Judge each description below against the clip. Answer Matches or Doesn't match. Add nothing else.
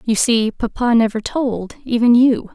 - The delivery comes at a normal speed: Matches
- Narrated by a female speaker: Matches